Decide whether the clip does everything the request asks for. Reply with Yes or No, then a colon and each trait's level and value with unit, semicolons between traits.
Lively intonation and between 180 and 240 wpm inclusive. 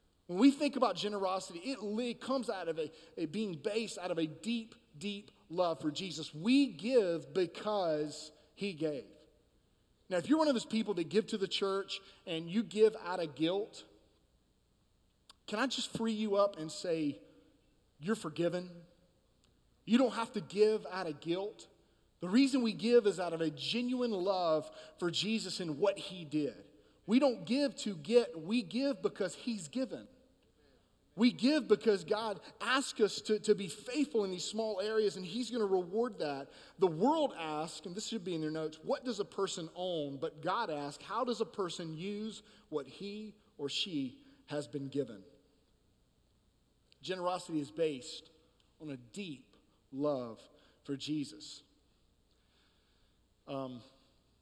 No: wide, 6.1 semitones; average, 165 wpm